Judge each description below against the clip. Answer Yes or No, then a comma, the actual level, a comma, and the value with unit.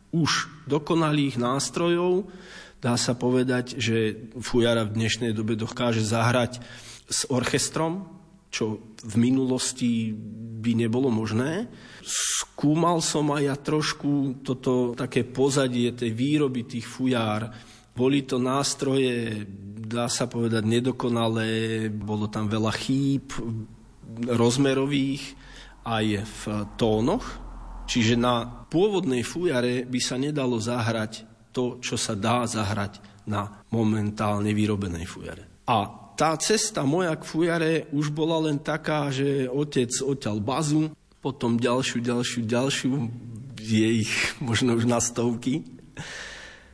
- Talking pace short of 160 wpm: Yes, average, 115 wpm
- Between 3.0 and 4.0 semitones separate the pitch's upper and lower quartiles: Yes, average, 3.5 semitones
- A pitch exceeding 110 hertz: Yes, low, 120 Hz